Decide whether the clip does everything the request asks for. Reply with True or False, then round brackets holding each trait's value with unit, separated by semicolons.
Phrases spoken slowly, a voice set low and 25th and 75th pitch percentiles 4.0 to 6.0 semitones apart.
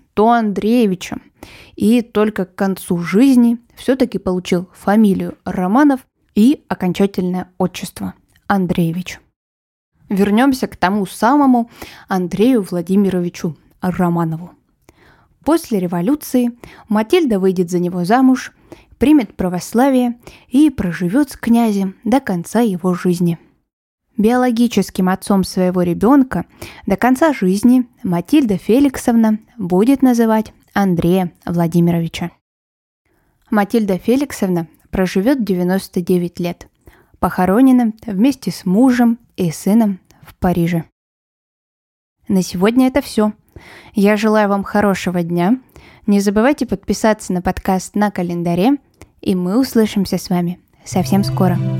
False (100 wpm; 200 Hz; 4.6 semitones)